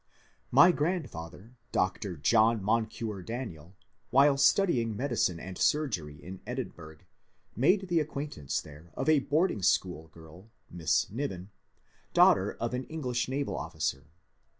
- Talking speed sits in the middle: No, slow, 125 wpm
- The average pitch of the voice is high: No, low, 110 Hz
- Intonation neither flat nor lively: No, wide, 8.2 semitones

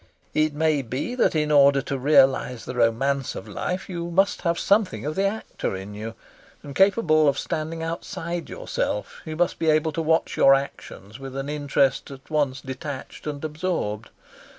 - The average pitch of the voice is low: No, medium, 150 Hz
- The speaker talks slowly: No, average, 175 wpm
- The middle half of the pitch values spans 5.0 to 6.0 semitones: No, average, 3.4 semitones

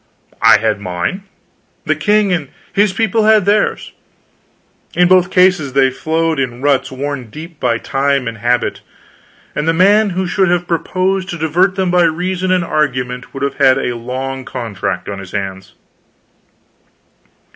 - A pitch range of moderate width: No, wide, 6.5 semitones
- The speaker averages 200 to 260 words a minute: No, average, 155 wpm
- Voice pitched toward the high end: No, medium, 155 Hz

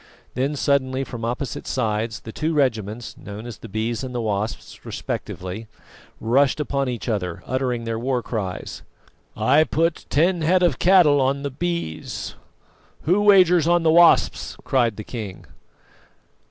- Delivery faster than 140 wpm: Yes, average, 150 wpm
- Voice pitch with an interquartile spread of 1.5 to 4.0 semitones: No, wide, 5.6 semitones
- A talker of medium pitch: No, low, 130 Hz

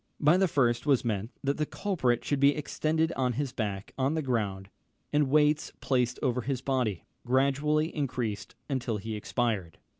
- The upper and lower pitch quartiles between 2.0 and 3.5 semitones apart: No, average, 3.9 semitones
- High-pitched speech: No, low, 130 Hz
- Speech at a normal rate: Yes, average, 170 wpm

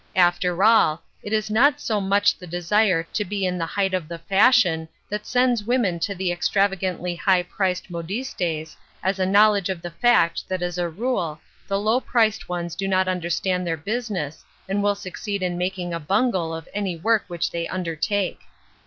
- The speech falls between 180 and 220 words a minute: Yes, average, 190 wpm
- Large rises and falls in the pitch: No, average, 3.0 semitones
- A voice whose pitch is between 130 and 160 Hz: No, medium, 185 Hz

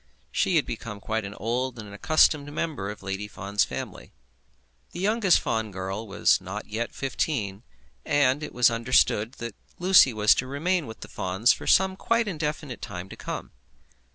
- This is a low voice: Yes, low, 115 Hz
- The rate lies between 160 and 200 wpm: Yes, average, 175 wpm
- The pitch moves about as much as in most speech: No, wide, 6.3 semitones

